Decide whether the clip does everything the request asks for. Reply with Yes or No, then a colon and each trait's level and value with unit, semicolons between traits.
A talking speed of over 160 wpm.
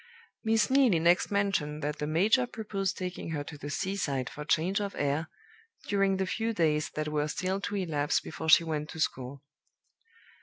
Yes: average, 180 wpm